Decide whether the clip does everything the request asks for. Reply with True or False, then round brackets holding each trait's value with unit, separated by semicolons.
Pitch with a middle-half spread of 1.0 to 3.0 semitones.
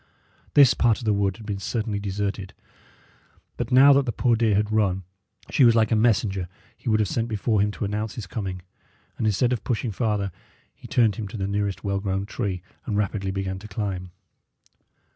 True (2.5 semitones)